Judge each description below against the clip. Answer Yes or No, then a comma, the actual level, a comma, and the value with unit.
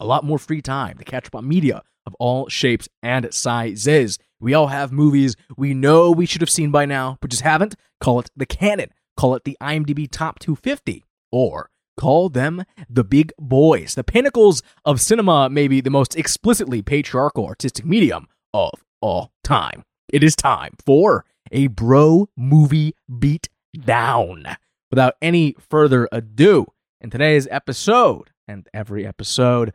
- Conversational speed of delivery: Yes, average, 160 wpm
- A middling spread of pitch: Yes, average, 3.7 semitones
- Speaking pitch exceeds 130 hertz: Yes, medium, 140 Hz